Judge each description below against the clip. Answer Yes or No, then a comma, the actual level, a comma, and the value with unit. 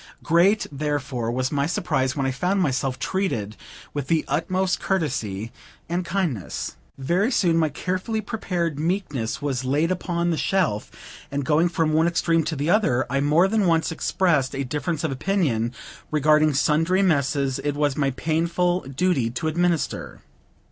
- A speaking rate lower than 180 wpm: Yes, average, 155 wpm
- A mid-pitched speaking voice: Yes, medium, 155 Hz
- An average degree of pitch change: Yes, average, 4.4 semitones